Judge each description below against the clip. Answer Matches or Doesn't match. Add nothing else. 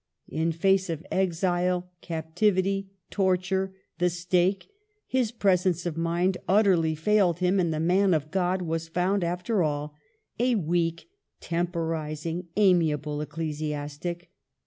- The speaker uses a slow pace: Matches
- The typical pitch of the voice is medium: Matches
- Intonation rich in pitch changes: Doesn't match